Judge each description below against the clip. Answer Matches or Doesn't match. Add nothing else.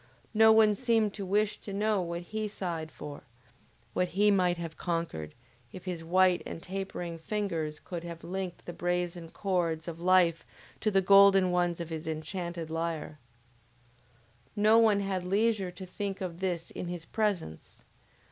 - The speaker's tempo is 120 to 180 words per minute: Matches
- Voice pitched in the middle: Matches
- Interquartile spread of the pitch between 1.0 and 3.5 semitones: Matches